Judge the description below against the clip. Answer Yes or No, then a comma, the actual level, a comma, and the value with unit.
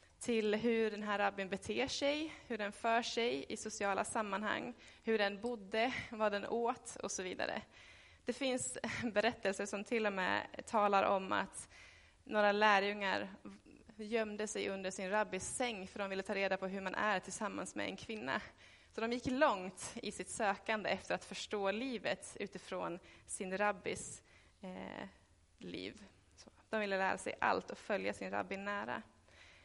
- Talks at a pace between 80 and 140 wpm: No, average, 160 wpm